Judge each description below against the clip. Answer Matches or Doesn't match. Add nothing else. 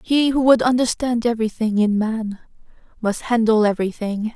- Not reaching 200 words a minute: Matches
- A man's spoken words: Doesn't match